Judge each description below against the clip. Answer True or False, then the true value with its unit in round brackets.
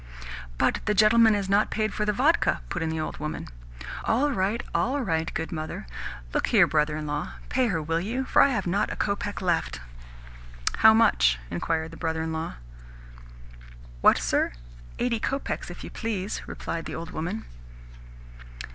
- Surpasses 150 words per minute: True (175 wpm)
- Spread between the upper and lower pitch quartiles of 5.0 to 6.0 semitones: True (5.6 semitones)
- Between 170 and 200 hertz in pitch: True (190 Hz)